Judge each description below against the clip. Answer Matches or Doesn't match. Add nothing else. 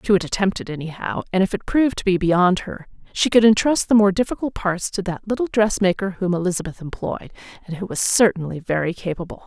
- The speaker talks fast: Matches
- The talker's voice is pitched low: Doesn't match